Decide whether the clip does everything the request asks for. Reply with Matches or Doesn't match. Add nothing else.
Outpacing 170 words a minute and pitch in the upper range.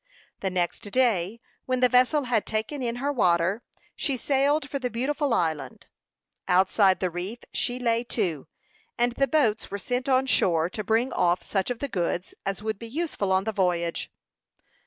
Matches